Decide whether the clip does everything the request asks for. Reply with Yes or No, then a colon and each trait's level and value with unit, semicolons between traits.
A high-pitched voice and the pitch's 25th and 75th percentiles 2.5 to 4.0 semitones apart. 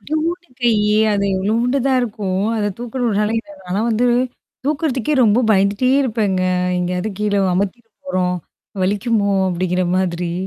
No: high, 210 Hz; average, 4.4 semitones